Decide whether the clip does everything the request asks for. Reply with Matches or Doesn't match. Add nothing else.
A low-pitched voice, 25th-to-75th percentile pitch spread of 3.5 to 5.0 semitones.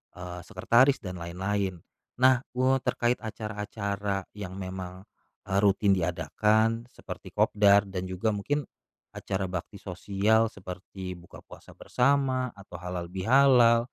Matches